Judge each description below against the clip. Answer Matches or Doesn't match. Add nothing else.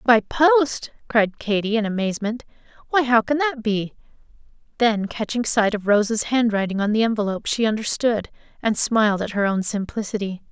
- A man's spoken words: Doesn't match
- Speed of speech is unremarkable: Matches